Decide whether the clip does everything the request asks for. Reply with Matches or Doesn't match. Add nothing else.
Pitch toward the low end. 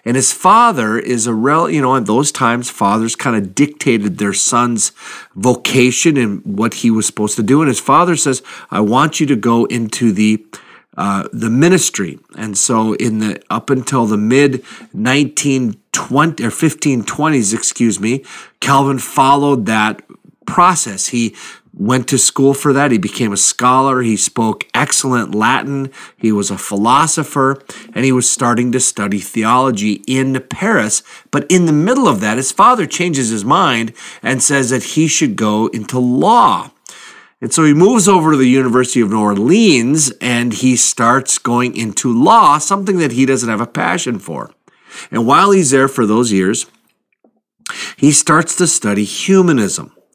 Matches